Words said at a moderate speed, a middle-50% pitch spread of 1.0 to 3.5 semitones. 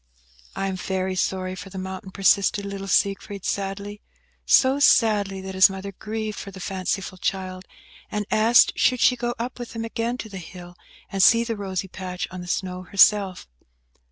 Yes: average, 180 wpm; narrow, 2.4 semitones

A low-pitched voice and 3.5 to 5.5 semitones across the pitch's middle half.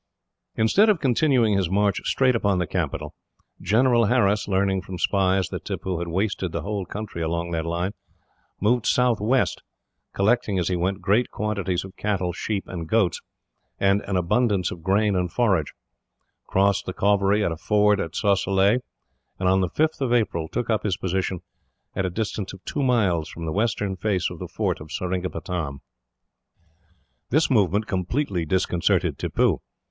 No: very low, 95 Hz; average, 3.0 semitones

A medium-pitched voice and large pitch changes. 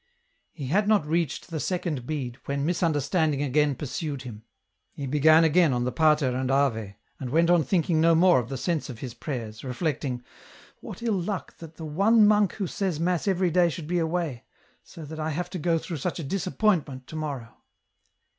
No: medium, 155 Hz; average, 4.4 semitones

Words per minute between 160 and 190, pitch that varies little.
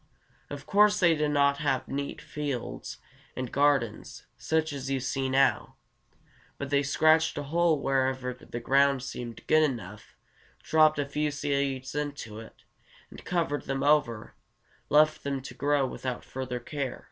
No: average, 150 wpm; narrow, 2.3 semitones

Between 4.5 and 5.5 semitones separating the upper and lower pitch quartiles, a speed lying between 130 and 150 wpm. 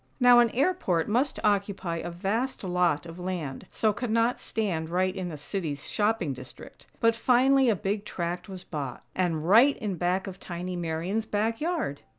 No: average, 4.8 semitones; average, 170 wpm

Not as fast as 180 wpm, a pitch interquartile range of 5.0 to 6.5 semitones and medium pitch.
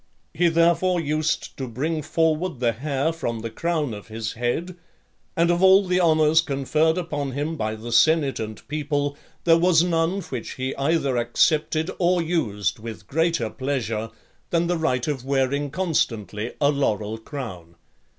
Yes: average, 160 wpm; wide, 5.4 semitones; medium, 145 Hz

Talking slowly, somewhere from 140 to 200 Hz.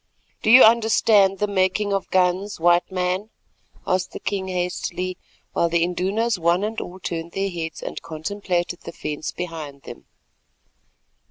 No: average, 150 wpm; medium, 185 Hz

